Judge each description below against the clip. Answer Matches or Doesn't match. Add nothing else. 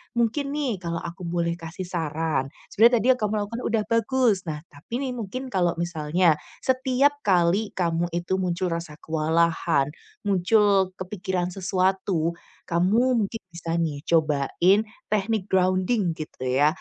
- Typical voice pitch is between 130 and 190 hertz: Matches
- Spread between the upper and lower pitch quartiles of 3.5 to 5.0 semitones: Matches